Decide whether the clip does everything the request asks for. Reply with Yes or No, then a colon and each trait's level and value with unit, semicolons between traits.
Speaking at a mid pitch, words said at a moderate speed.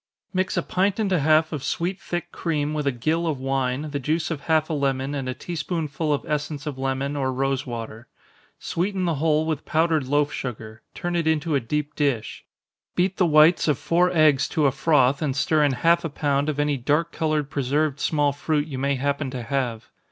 No: medium, 150 Hz; fast, 215 wpm